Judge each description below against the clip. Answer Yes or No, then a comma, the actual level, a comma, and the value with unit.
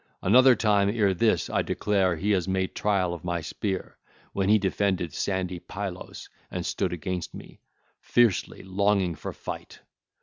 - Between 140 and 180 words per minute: Yes, average, 155 wpm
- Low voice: Yes, very low, 95 Hz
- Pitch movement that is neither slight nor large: No, narrow, 2.2 semitones